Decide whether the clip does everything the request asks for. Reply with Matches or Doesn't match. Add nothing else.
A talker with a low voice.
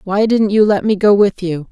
Doesn't match